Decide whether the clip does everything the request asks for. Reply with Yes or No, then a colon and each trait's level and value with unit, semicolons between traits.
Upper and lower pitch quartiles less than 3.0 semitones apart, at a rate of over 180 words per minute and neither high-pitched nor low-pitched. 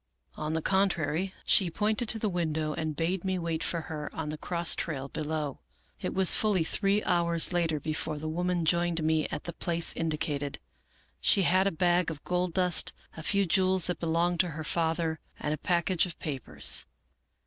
Yes: narrow, 2.4 semitones; average, 190 wpm; medium, 170 Hz